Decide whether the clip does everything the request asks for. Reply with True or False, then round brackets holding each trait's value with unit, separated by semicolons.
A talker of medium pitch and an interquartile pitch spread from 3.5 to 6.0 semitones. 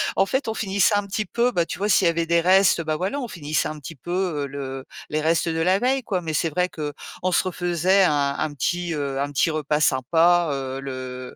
True (165 Hz; 4.3 semitones)